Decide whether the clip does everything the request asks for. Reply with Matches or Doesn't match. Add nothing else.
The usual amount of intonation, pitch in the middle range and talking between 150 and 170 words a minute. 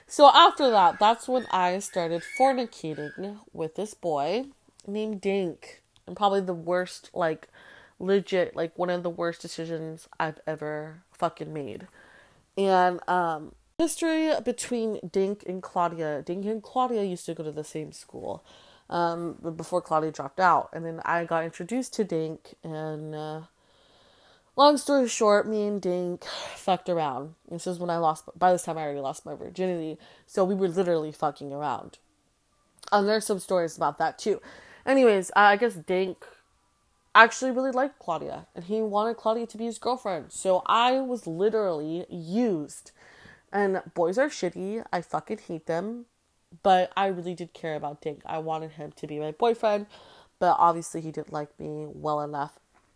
Matches